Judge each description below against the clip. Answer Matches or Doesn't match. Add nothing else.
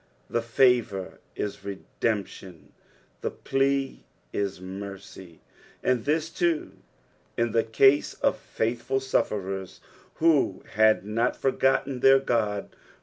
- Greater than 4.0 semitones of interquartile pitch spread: Matches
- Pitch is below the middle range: Matches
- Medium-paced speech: Doesn't match